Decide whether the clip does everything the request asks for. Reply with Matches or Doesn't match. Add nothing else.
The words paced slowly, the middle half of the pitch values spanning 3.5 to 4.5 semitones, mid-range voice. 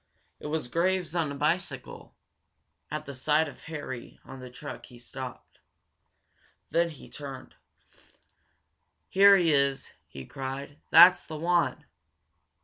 Matches